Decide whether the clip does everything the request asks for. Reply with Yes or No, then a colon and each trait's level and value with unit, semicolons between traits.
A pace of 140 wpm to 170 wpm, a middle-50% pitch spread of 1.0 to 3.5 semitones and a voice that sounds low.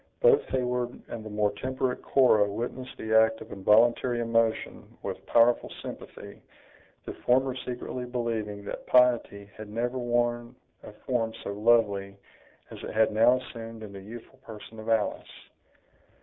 Yes: average, 150 wpm; narrow, 2.4 semitones; low, 115 Hz